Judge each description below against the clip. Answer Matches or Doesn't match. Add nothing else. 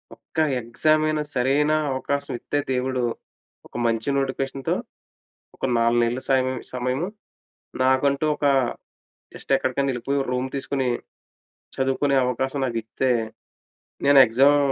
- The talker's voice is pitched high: Doesn't match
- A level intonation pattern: Matches